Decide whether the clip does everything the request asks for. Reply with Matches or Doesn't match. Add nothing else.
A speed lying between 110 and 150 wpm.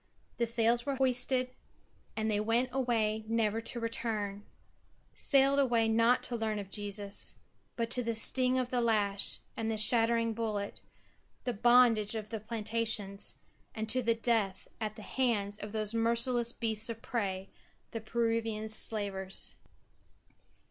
Matches